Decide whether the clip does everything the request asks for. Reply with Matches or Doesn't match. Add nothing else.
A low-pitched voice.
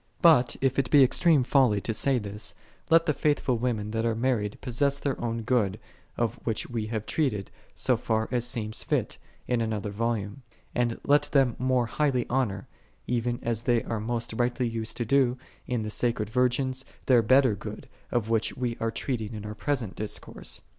Matches